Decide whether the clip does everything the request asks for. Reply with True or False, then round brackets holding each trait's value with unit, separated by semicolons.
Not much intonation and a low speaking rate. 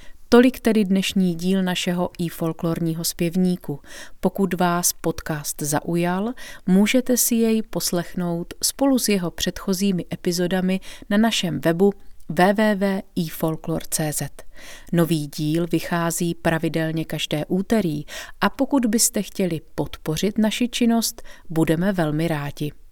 False (3.7 semitones; 105 wpm)